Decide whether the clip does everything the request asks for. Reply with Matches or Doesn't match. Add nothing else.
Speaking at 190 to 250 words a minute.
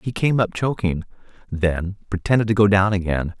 Doesn't match